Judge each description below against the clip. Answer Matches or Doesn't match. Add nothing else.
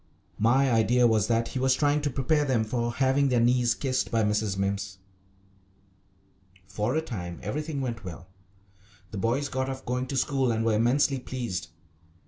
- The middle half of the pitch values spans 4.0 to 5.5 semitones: Doesn't match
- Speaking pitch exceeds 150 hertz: Doesn't match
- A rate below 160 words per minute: Doesn't match